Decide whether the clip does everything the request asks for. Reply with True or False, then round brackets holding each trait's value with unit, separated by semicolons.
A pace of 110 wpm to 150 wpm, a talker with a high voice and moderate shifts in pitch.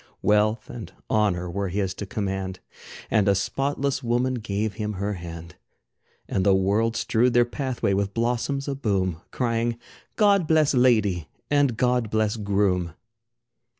False (140 wpm; 105 Hz; 4.1 semitones)